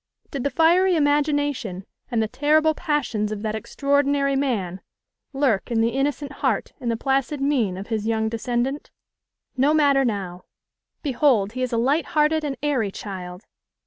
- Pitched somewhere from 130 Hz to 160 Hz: No, very high, 265 Hz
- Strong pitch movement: No, average, 4.7 semitones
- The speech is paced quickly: No, average, 160 wpm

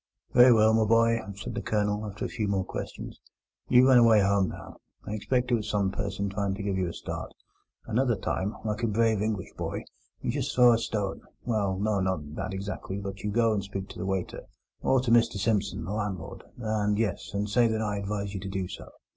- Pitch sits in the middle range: No, low, 105 Hz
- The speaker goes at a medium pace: No, fast, 215 wpm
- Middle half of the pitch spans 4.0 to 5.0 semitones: No, narrow, 2.6 semitones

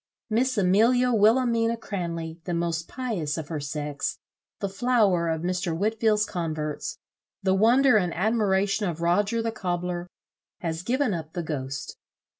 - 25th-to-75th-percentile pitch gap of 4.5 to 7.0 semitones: Yes, average, 5.1 semitones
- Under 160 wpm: Yes, average, 140 wpm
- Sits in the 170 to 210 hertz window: Yes, high, 190 Hz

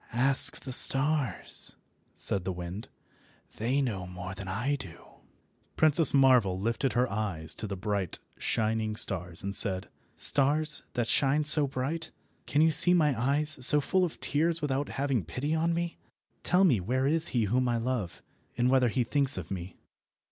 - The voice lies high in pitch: No, low, 130 Hz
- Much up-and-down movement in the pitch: Yes, wide, 6.3 semitones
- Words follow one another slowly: No, average, 170 wpm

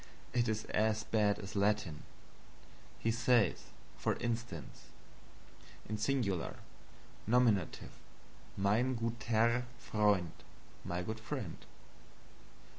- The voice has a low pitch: Yes, low, 110 Hz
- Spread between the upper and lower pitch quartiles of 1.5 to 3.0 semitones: Yes, narrow, 2.6 semitones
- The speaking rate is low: Yes, slow, 85 wpm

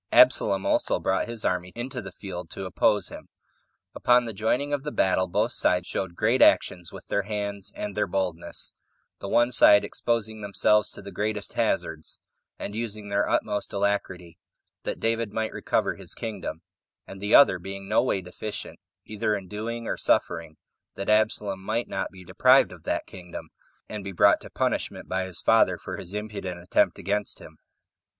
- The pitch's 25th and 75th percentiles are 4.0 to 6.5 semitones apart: No, average, 2.7 semitones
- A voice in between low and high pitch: No, low, 100 Hz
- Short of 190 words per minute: Yes, average, 175 wpm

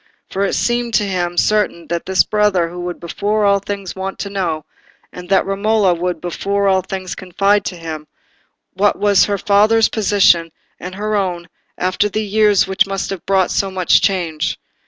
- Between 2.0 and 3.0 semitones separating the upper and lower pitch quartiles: Yes, narrow, 2.4 semitones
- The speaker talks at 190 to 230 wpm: No, average, 180 wpm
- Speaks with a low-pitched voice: No, high, 195 Hz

